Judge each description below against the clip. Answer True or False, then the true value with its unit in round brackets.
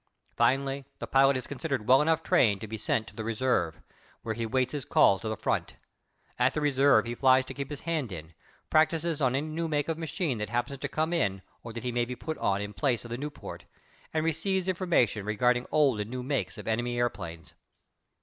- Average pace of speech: False (220 wpm)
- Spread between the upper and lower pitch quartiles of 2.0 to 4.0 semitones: False (4.9 semitones)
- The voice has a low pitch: True (130 Hz)